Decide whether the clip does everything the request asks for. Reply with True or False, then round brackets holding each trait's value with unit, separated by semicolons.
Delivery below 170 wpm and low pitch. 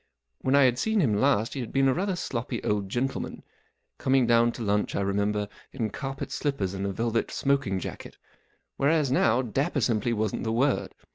False (185 wpm; 120 Hz)